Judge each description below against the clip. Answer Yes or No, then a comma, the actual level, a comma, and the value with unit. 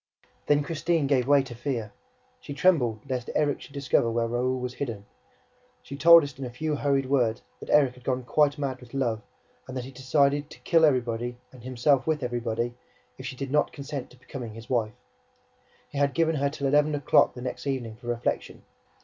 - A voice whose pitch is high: No, low, 130 Hz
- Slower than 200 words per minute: No, fast, 205 wpm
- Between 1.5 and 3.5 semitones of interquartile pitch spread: Yes, average, 2.9 semitones